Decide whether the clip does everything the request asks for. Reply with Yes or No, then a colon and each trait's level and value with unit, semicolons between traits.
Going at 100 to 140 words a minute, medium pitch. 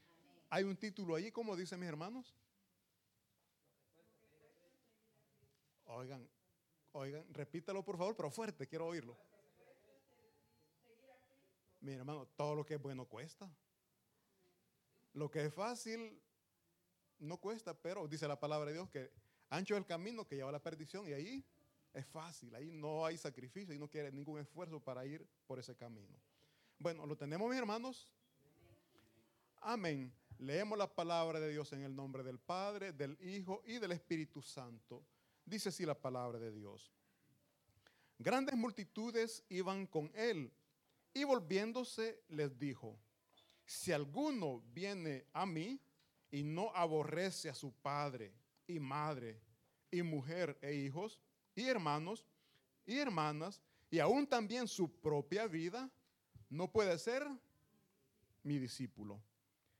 Yes: average, 135 wpm; medium, 155 Hz